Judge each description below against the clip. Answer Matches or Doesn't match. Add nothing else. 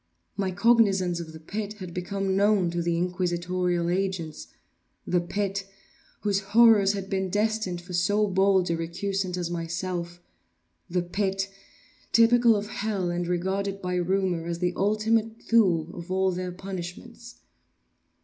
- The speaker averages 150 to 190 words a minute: Doesn't match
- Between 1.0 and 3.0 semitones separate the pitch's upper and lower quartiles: Matches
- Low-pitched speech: Doesn't match